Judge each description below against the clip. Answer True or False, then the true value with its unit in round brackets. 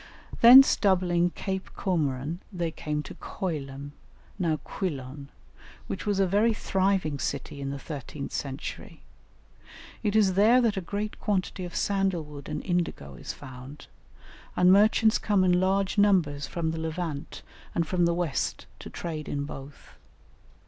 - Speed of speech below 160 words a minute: True (150 wpm)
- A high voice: False (175 Hz)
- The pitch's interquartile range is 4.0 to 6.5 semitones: True (5.0 semitones)